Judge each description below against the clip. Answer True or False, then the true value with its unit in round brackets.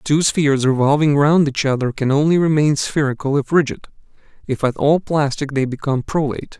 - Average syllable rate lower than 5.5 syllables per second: False (5.7 syllables/s)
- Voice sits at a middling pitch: True (145 Hz)